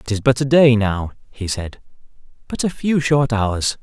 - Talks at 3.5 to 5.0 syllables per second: Yes, 4.5 syllables/s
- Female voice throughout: No, male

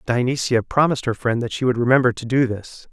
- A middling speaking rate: No, fast, 225 wpm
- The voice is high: No, low, 125 Hz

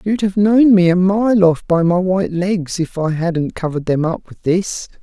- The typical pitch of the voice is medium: Yes, medium, 180 Hz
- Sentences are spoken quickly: Yes, fast, 225 wpm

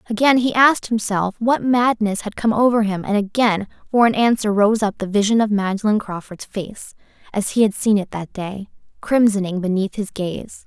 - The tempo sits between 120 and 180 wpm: No, average, 190 wpm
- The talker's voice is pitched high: Yes, high, 210 Hz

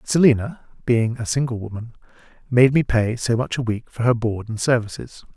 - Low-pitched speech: Yes, low, 120 Hz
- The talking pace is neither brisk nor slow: Yes, average, 190 wpm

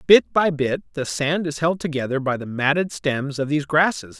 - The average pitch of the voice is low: No, medium, 150 Hz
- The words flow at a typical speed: No, fast, 215 wpm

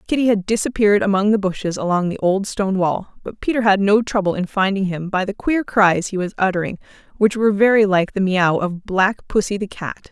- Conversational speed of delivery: No, fast, 220 wpm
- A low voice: No, high, 200 Hz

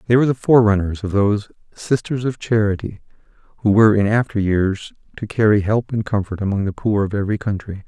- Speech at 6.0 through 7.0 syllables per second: Yes, 6.3 syllables/s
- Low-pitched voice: Yes, low, 105 Hz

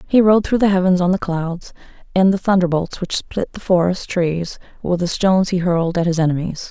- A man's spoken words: No, female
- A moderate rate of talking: No, fast, 215 wpm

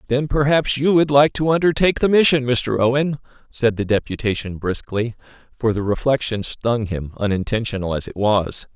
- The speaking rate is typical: Yes, average, 165 wpm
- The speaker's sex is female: No, male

